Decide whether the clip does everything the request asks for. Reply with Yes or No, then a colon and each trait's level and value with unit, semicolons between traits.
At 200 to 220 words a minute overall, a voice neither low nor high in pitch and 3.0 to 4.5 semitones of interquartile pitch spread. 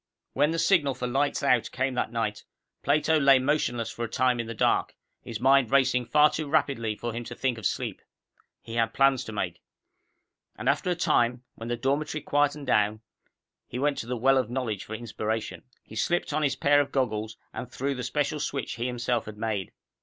No: fast, 205 wpm; low, 125 Hz; average, 3.5 semitones